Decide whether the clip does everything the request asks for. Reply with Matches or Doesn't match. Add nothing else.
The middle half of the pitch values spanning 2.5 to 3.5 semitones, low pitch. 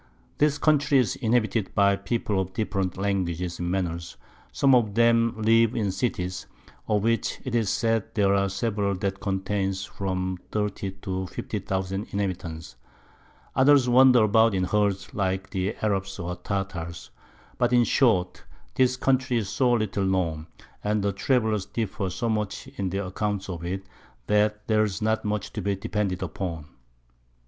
Matches